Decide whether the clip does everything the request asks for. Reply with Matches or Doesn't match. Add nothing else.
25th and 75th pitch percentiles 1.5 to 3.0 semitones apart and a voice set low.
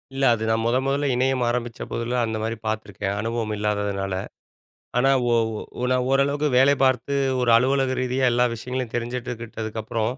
Matches